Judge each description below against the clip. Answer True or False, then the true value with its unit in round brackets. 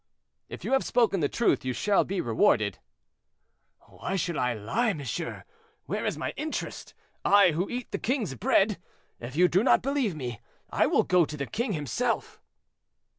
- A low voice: False (180 Hz)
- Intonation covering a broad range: True (8.2 semitones)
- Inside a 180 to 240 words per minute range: False (170 wpm)